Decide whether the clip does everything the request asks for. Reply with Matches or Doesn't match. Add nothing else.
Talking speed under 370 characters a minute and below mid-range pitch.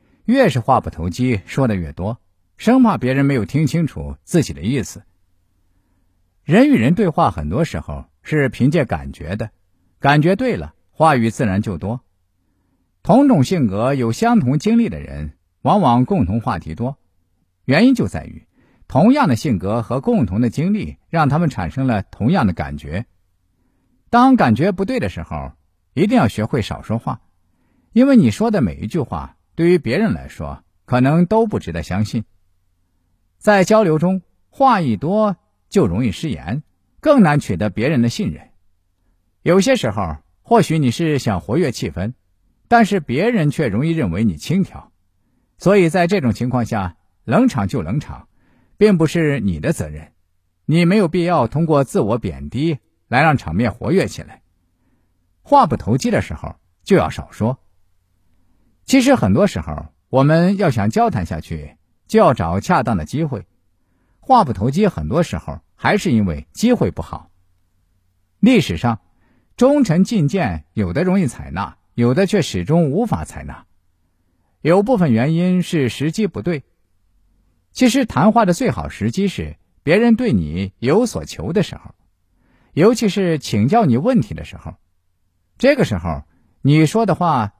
Matches